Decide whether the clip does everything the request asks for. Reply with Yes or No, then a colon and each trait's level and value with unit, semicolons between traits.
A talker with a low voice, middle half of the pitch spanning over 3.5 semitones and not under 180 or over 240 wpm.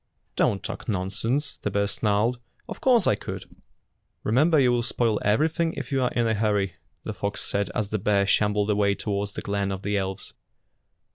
No: low, 105 Hz; average, 3.2 semitones; average, 190 wpm